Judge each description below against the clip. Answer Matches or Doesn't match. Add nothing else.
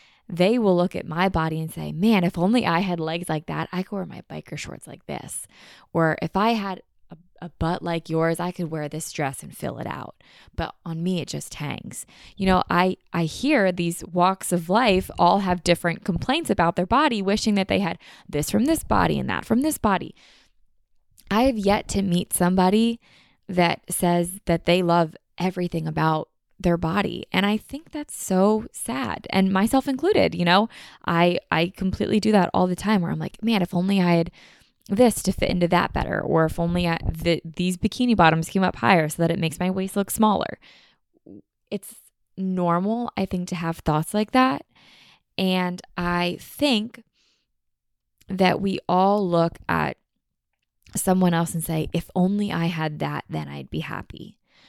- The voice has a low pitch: Doesn't match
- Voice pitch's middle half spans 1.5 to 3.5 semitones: Matches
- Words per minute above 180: Matches